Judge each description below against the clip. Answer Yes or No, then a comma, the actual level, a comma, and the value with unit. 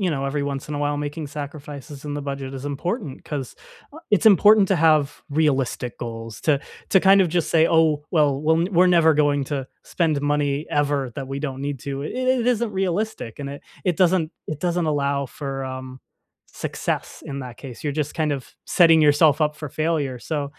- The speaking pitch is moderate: Yes, medium, 145 Hz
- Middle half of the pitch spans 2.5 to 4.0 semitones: Yes, average, 2.9 semitones